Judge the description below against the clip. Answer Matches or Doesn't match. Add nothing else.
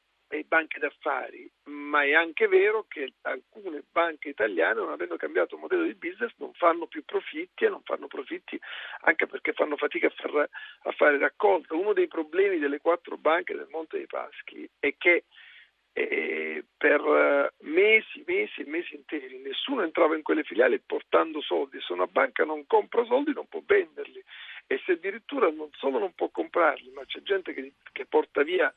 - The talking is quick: Matches